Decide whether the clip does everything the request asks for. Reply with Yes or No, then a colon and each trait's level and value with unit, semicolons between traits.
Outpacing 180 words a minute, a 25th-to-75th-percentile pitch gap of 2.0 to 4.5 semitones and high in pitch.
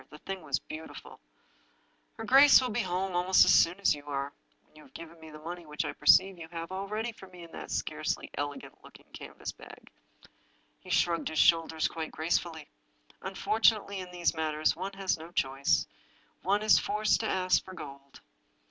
No: average, 200 wpm; average, 3.7 semitones; medium, 170 Hz